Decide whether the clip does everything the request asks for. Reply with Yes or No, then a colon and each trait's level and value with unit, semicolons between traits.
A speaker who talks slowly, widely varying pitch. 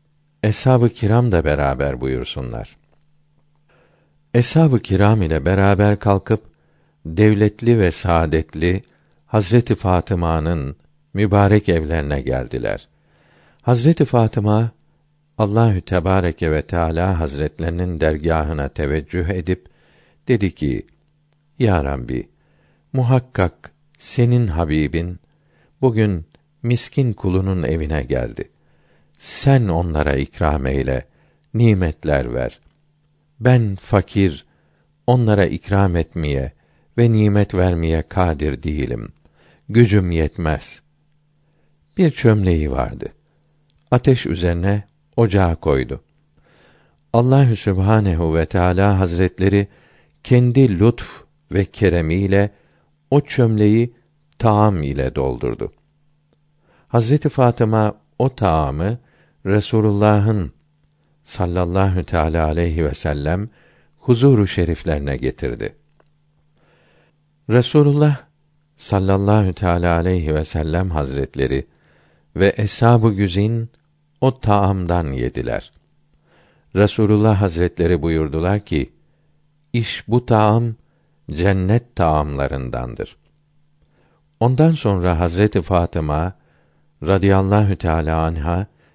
Yes: slow, 80 wpm; wide, 7.1 semitones